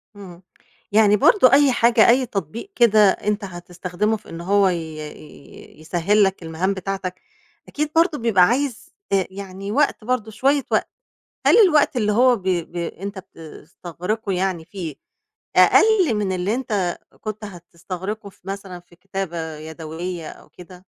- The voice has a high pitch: Yes, high, 195 Hz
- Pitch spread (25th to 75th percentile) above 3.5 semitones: Yes, average, 3.9 semitones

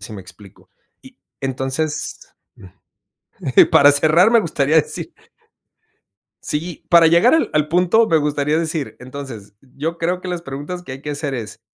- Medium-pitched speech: Yes, medium, 150 Hz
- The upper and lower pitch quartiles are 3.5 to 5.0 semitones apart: Yes, average, 3.9 semitones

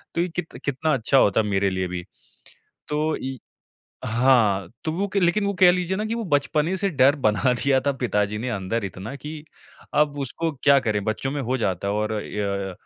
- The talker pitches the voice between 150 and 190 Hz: No, low, 130 Hz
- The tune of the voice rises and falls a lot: Yes, wide, 6.8 semitones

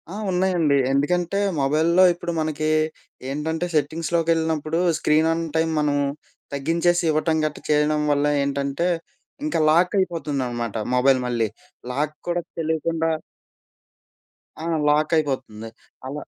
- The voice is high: No, medium, 155 Hz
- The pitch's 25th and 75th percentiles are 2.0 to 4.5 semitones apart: Yes, average, 2.8 semitones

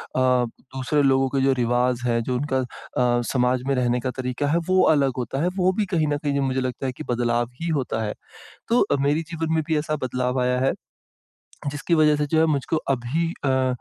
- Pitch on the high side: No, low, 130 Hz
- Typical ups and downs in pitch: Yes, average, 3.1 semitones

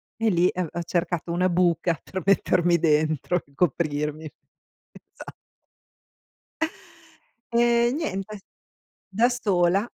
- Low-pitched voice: No, medium, 175 Hz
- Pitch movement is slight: No, average, 3.1 semitones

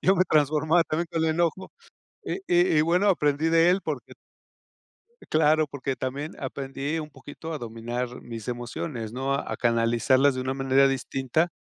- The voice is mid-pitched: Yes, medium, 145 Hz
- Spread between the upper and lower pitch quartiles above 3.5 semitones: Yes, average, 3.9 semitones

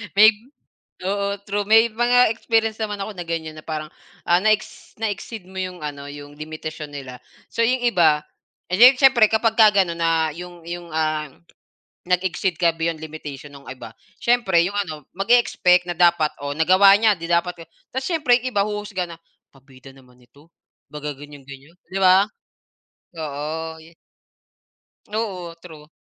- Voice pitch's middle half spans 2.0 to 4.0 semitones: No, average, 5.2 semitones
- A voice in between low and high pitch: Yes, medium, 175 Hz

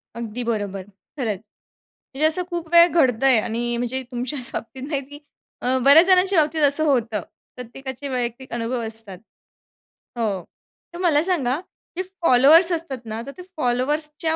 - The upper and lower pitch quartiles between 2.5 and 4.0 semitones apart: No, average, 4.6 semitones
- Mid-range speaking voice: No, very high, 265 Hz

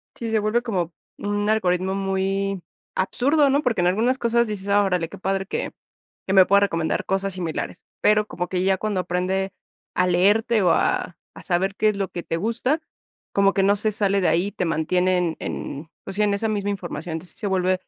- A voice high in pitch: Yes, high, 195 Hz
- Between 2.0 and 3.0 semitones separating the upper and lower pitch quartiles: Yes, narrow, 2.6 semitones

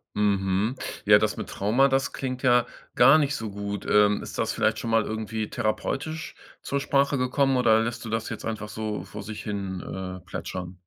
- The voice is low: Yes, low, 110 Hz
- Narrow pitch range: No, average, 3.8 semitones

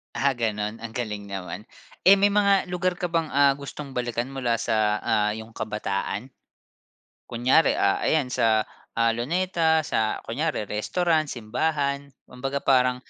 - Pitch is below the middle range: Yes, low, 125 Hz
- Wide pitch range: Yes, wide, 6.1 semitones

